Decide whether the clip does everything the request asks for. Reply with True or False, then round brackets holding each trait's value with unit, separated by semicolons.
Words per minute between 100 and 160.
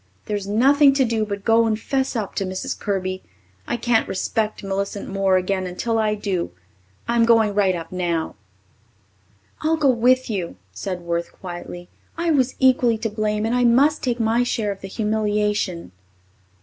False (170 wpm)